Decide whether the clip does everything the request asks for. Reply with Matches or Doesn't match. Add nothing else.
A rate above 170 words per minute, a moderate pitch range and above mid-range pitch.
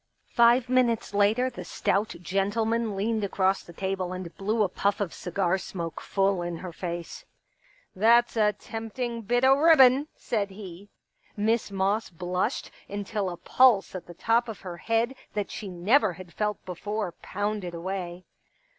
Doesn't match